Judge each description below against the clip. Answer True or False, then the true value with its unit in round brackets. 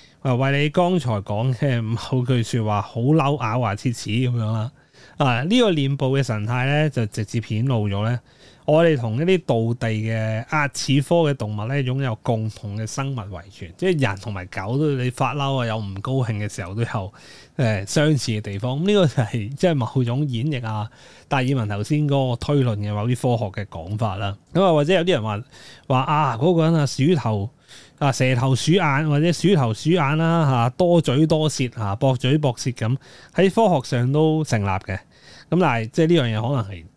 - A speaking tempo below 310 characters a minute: True (295 characters per minute)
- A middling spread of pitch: True (5.0 semitones)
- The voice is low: True (130 Hz)